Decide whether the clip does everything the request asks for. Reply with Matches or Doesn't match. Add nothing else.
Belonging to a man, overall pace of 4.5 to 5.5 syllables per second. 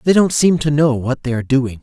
Doesn't match